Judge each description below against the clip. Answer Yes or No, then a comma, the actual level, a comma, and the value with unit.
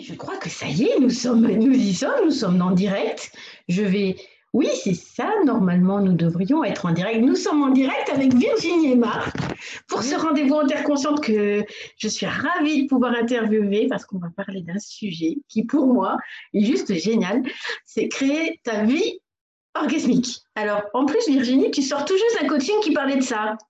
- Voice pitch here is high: Yes, very high, 250 Hz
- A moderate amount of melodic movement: No, wide, 6.0 semitones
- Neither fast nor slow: Yes, average, 200 wpm